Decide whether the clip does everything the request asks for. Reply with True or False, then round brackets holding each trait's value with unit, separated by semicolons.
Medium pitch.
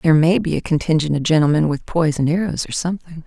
True (160 Hz)